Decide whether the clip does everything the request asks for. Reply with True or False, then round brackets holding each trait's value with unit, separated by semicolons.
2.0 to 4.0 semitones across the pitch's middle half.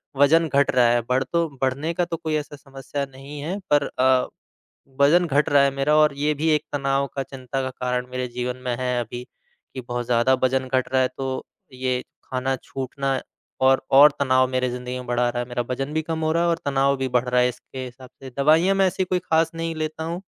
True (3.1 semitones)